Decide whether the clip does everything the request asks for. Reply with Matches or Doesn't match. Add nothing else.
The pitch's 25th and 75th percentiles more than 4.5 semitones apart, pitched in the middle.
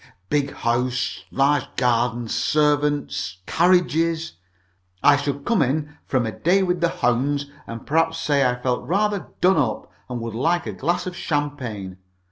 Matches